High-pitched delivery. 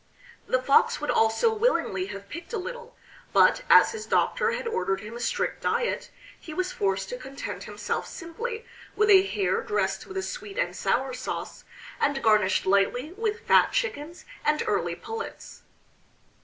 Yes: very high, 335 Hz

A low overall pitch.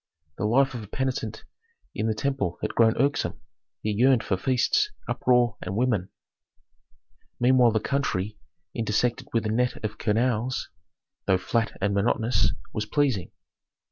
Yes: low, 115 Hz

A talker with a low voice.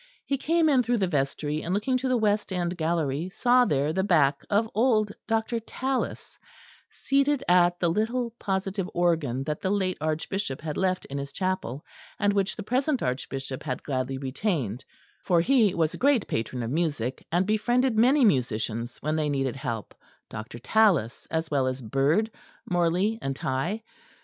No: medium, 175 Hz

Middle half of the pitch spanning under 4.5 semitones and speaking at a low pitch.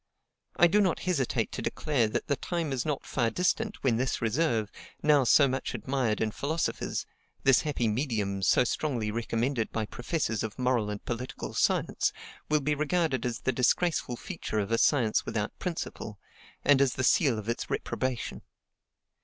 No: average, 4.9 semitones; low, 130 Hz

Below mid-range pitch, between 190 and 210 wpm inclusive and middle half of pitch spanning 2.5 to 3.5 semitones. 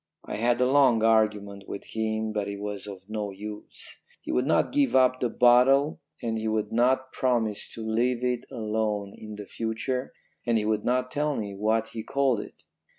Yes: low, 110 Hz; average, 195 wpm; average, 3.0 semitones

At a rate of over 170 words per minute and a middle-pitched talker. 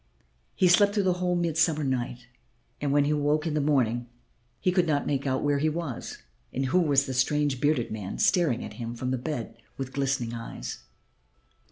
Yes: average, 200 wpm; medium, 145 Hz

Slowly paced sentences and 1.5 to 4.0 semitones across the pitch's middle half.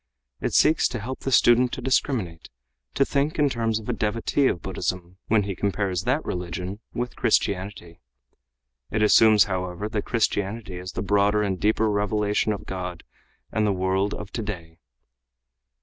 No: average, 160 wpm; average, 3.2 semitones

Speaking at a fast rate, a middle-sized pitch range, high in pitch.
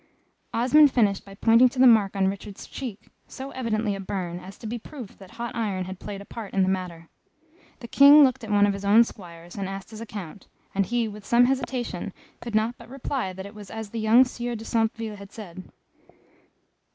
Yes: fast, 215 wpm; average, 3.4 semitones; high, 215 Hz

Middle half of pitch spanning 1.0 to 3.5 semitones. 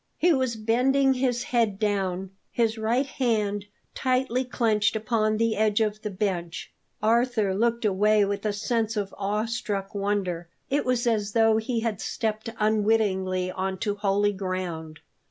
Yes: average, 2.7 semitones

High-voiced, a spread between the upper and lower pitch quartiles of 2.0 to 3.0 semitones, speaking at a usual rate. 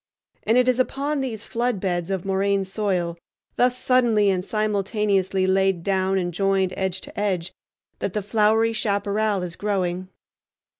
Yes: high, 200 Hz; narrow, 2.5 semitones; average, 150 wpm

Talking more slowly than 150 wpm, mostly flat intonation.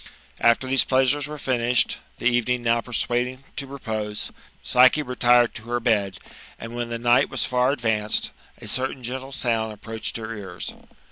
No: average, 165 wpm; narrow, 2.2 semitones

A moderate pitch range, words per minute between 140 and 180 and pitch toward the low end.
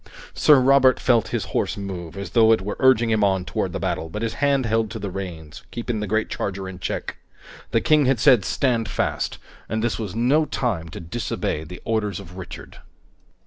No: average, 4.2 semitones; fast, 205 wpm; low, 110 Hz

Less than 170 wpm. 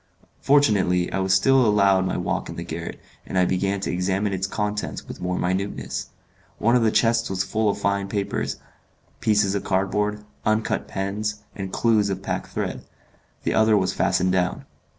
No: average, 175 wpm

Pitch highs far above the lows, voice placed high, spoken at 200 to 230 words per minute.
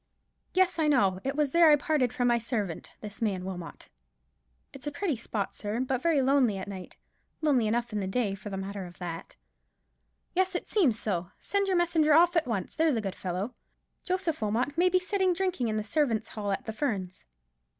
Yes: wide, 7.6 semitones; high, 245 Hz; fast, 205 wpm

